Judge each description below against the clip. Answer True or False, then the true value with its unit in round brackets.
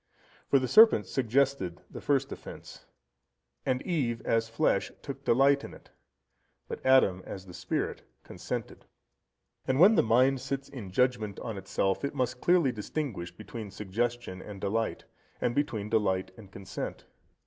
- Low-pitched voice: True (115 Hz)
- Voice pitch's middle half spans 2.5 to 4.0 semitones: False (5.1 semitones)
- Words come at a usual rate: True (150 wpm)